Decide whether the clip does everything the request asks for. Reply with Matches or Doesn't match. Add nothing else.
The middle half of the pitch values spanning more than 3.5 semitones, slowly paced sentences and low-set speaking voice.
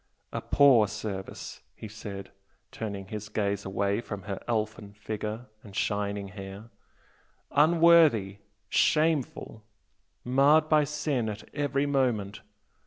Matches